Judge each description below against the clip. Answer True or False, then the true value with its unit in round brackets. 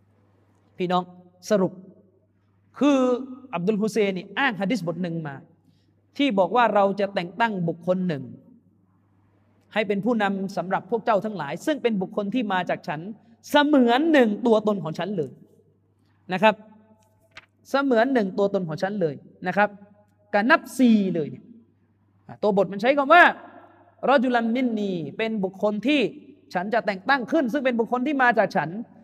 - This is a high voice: True (200 Hz)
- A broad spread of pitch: True (5.8 semitones)